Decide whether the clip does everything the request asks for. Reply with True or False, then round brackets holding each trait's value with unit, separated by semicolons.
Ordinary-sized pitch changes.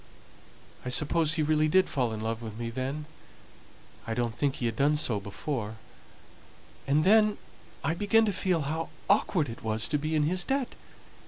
False (6.1 semitones)